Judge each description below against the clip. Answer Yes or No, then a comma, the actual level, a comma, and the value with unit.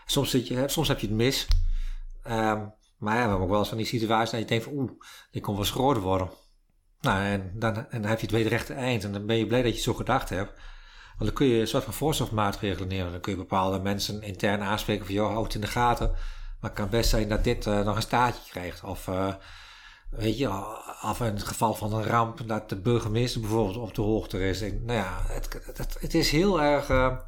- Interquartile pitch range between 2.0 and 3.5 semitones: Yes, average, 3.0 semitones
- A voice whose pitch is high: No, low, 110 Hz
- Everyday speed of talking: No, fast, 250 wpm